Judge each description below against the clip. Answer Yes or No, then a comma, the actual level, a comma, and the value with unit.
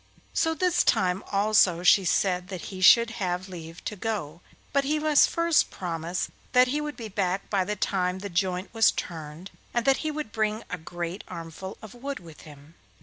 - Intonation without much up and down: No, average, 4.8 semitones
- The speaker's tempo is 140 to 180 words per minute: No, average, 195 wpm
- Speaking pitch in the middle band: No, high, 195 Hz